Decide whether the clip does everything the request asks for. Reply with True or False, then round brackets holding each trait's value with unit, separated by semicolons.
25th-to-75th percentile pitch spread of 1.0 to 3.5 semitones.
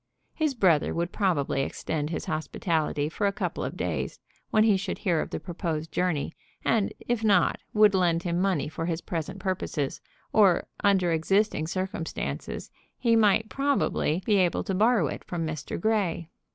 False (4.1 semitones)